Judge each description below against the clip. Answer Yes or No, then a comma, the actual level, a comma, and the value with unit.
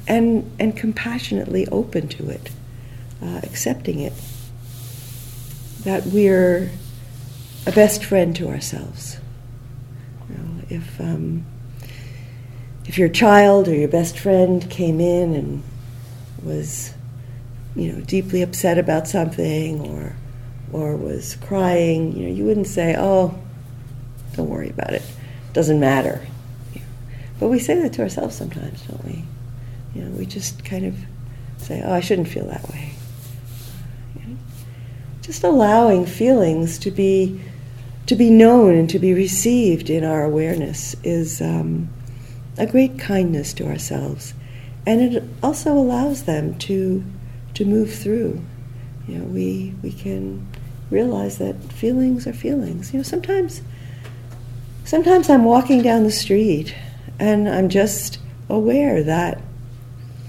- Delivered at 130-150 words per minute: Yes, slow, 135 wpm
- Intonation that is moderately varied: No, wide, 7.1 semitones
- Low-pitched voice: Yes, low, 130 Hz